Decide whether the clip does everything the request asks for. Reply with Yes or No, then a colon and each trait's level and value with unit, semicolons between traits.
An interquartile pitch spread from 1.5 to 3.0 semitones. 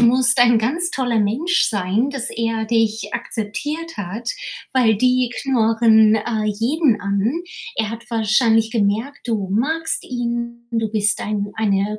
Yes: narrow, 2.6 semitones